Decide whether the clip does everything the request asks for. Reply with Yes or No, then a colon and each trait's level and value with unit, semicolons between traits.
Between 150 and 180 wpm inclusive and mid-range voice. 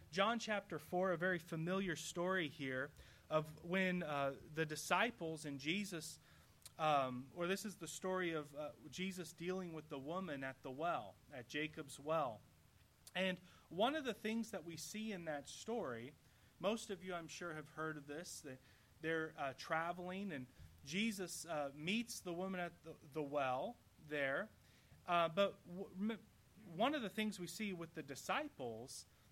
Yes: average, 165 wpm; medium, 170 Hz